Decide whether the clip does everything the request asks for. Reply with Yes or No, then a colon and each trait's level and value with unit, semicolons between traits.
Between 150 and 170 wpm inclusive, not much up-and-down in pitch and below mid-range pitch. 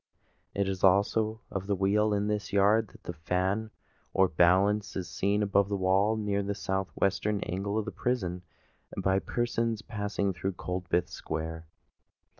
Yes: average, 160 wpm; narrow, 2.0 semitones; low, 100 Hz